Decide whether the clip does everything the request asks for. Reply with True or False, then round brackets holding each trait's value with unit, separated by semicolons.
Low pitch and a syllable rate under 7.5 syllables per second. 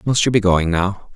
True (100 Hz; 5.0 syllables/s)